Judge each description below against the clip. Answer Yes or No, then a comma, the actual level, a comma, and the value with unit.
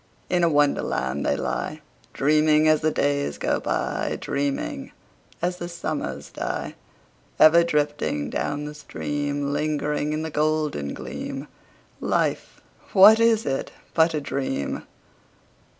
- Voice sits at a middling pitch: Yes, medium, 150 Hz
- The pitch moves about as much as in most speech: No, narrow, 1.8 semitones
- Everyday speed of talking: No, slow, 125 wpm